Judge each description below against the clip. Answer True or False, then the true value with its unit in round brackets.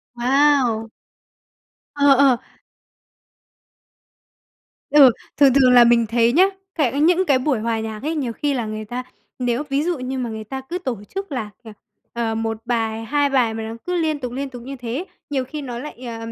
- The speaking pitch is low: False (255 Hz)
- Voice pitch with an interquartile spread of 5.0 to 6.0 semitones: False (3.8 semitones)